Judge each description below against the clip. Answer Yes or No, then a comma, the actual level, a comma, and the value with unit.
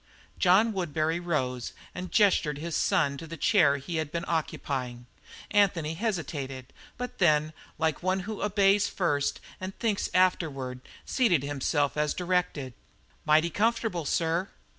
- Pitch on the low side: No, medium, 165 Hz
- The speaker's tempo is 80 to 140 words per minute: Yes, slow, 135 wpm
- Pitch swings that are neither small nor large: Yes, average, 4.5 semitones